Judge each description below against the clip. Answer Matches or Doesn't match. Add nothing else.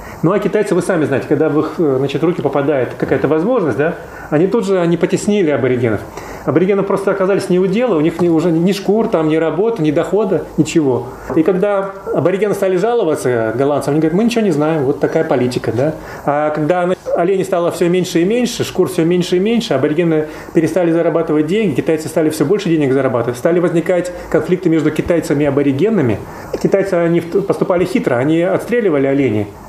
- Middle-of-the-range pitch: Matches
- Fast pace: Matches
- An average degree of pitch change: Matches